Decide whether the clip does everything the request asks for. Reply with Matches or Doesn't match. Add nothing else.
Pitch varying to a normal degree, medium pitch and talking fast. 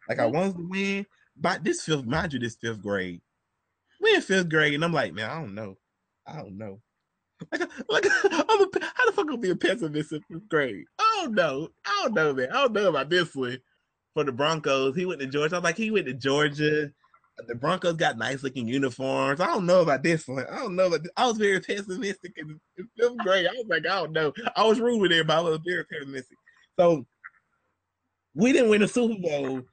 Doesn't match